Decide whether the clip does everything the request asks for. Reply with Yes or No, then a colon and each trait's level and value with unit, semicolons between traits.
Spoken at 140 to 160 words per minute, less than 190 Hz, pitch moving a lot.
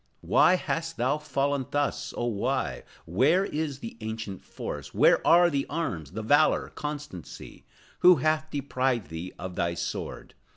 Yes: average, 150 wpm; low, 135 Hz; wide, 5.8 semitones